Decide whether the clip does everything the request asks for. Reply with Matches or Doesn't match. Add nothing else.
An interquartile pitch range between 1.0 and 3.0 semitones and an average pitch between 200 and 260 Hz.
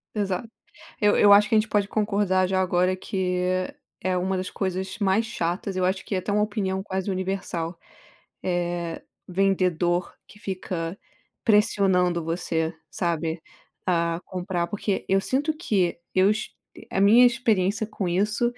Doesn't match